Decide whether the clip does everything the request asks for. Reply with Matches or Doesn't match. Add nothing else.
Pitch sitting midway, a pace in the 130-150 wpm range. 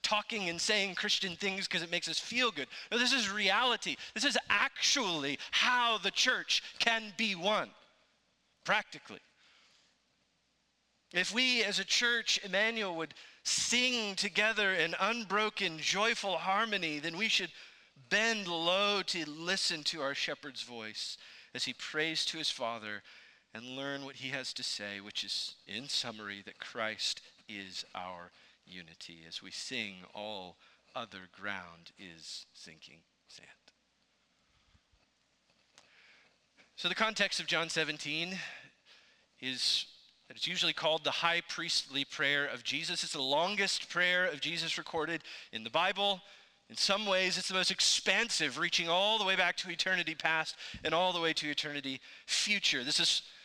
Matches